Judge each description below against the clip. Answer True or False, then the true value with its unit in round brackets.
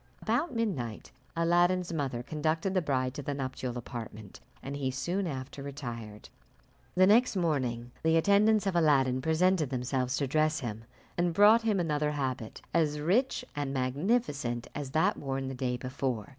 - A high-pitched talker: False (145 Hz)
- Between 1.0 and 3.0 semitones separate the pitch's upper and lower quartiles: False (5.3 semitones)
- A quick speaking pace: False (155 wpm)